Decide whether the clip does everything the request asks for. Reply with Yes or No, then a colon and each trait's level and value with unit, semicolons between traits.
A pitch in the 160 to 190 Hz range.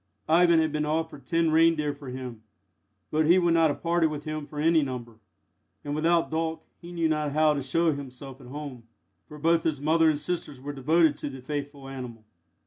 No: medium, 150 Hz